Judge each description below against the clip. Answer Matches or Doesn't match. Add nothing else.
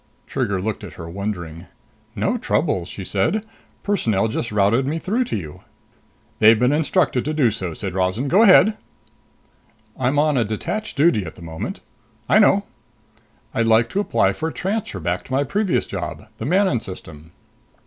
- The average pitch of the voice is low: Matches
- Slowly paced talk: Doesn't match